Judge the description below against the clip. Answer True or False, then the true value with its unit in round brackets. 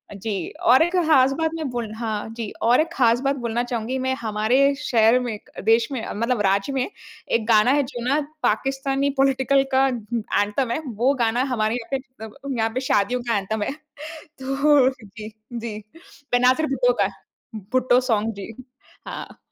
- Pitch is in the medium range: False (245 Hz)